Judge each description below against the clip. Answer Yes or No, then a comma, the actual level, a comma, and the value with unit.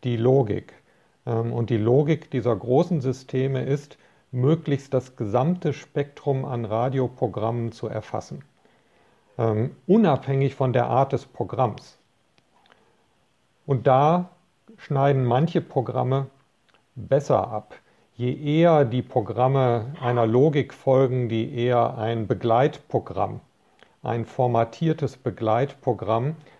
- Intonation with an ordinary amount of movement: Yes, average, 3.1 semitones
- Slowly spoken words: Yes, slow, 100 wpm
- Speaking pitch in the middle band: No, low, 130 Hz